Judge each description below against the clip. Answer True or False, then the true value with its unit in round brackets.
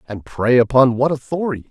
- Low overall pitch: True (130 Hz)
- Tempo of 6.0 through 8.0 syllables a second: False (5.8 syllables/s)